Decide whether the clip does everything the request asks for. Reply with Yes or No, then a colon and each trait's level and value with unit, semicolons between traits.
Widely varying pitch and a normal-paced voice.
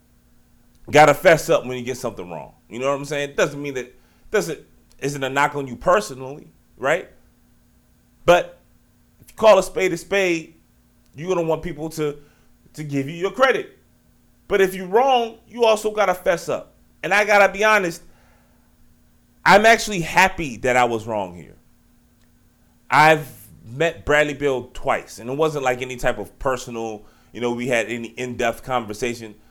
Yes: wide, 5.8 semitones; average, 180 wpm